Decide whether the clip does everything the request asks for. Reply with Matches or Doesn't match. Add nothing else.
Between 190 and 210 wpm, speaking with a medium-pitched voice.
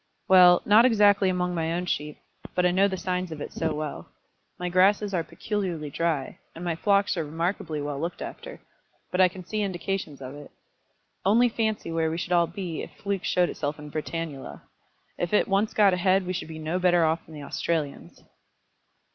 Matches